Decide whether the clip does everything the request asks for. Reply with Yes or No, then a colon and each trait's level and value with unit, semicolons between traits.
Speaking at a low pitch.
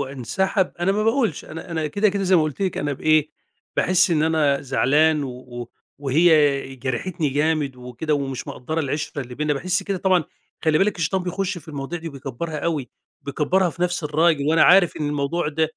No: medium, 155 Hz